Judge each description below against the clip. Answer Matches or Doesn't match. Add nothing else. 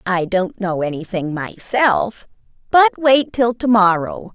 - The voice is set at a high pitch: Matches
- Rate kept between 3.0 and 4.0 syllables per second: Matches